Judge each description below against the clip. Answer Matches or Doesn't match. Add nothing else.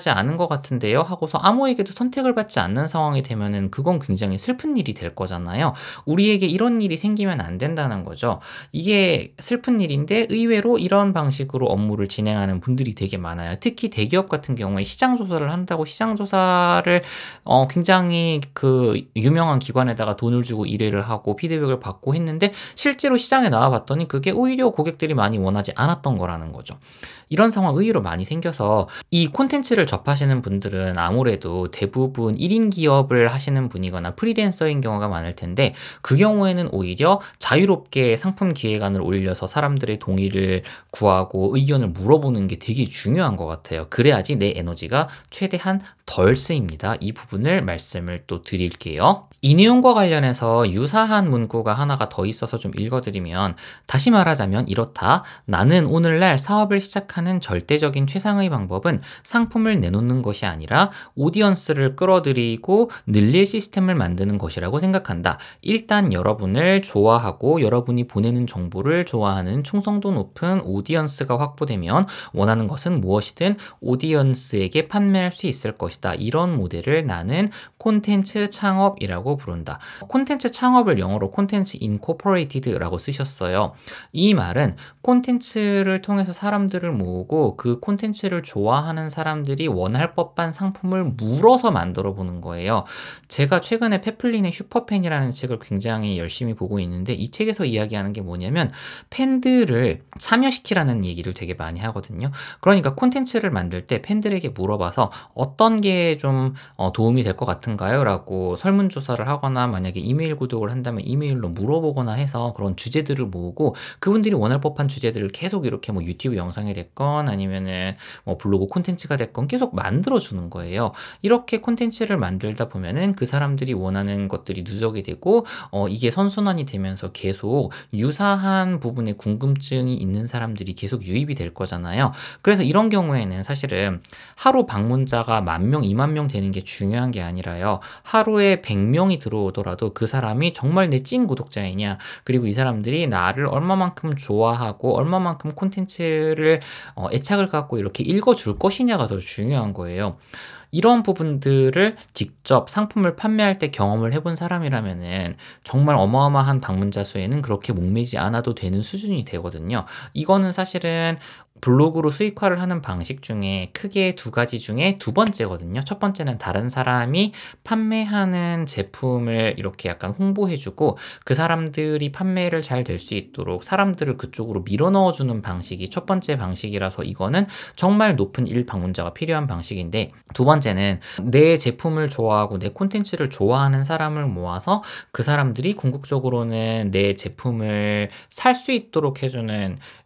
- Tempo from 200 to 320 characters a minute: Doesn't match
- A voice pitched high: Doesn't match